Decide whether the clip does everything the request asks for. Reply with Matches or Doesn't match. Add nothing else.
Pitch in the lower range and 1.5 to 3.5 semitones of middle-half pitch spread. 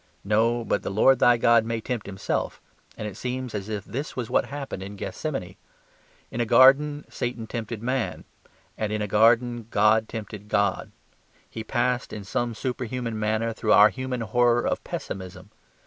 Matches